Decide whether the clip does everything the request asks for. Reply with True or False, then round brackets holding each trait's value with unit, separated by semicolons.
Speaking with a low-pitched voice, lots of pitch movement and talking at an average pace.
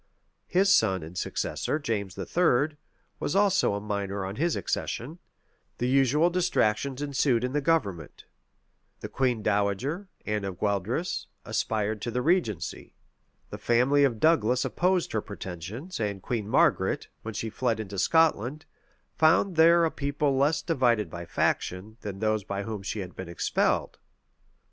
True (120 Hz; 7.0 semitones; 150 wpm)